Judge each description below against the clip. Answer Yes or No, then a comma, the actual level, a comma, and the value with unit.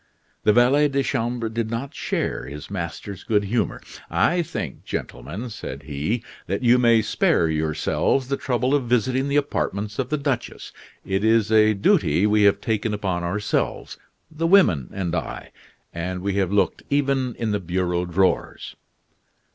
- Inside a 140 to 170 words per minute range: Yes, average, 160 wpm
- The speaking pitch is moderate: No, low, 110 Hz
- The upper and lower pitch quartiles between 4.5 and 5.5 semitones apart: Yes, average, 5.2 semitones